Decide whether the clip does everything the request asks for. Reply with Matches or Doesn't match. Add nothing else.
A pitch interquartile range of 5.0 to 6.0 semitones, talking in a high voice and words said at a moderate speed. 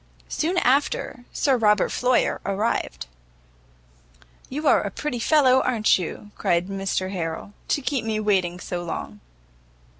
Doesn't match